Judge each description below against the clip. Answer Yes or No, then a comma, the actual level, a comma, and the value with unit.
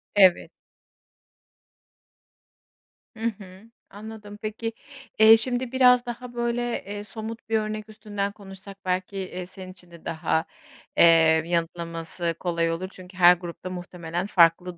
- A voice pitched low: No, high, 190 Hz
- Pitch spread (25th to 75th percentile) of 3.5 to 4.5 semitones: Yes, average, 3.9 semitones